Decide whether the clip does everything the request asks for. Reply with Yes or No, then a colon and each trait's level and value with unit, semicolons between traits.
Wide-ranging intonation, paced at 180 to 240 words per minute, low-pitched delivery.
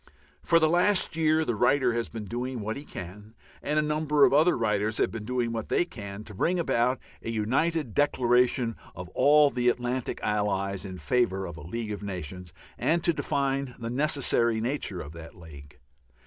Yes: wide, 5.7 semitones; average, 190 wpm; low, 120 Hz